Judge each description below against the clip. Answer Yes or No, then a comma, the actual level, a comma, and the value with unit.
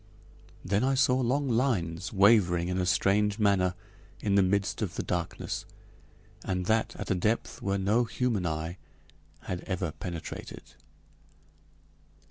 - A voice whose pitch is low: Yes, low, 100 Hz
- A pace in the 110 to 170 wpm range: Yes, slow, 135 wpm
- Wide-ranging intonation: No, average, 3.8 semitones